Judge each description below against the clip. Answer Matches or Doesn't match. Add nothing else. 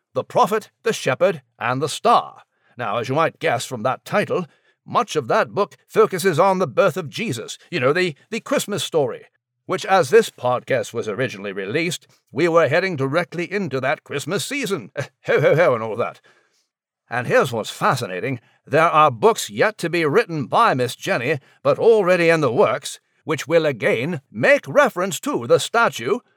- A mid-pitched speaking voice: Matches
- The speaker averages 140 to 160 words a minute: Doesn't match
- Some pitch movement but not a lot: Doesn't match